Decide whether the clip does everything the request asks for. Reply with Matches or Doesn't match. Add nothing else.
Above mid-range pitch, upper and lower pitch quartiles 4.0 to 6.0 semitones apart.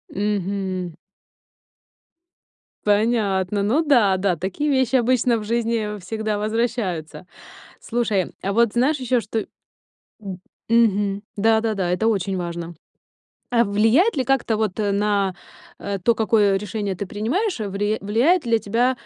Doesn't match